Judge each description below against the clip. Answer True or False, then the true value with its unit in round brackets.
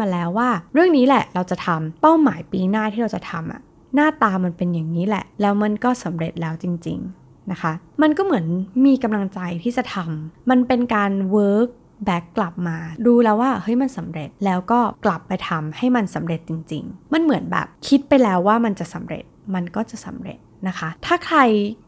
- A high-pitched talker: True (205 Hz)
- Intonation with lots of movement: True (5.8 semitones)